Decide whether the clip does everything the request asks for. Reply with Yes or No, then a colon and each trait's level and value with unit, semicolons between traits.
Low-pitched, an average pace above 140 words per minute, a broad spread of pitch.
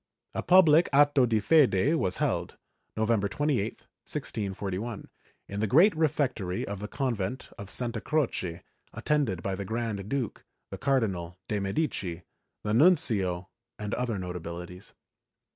No: low, 110 Hz; slow, 135 wpm; wide, 6.3 semitones